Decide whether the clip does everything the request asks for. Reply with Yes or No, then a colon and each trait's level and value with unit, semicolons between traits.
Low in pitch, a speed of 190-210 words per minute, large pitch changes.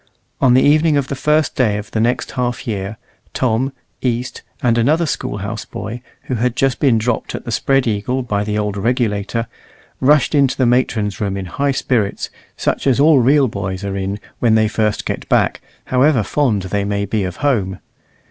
No: low, 120 Hz; average, 195 wpm; average, 4.3 semitones